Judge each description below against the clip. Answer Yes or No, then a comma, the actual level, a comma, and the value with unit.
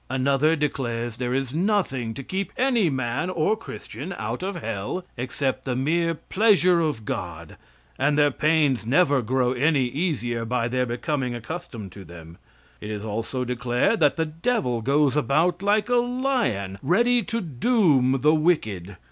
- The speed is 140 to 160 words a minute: Yes, average, 155 wpm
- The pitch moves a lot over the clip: Yes, wide, 6.4 semitones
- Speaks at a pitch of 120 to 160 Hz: Yes, low, 135 Hz